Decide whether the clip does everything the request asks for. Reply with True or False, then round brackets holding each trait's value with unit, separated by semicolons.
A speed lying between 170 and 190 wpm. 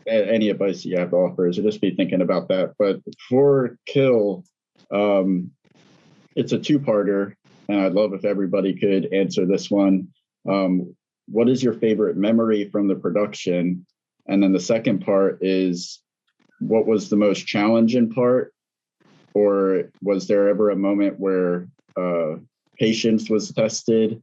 False (155 wpm)